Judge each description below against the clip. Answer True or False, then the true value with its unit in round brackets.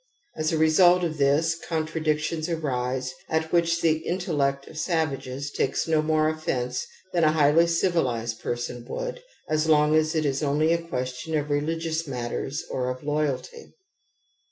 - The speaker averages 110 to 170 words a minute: True (155 wpm)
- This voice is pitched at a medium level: True (155 Hz)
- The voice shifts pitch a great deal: False (2.9 semitones)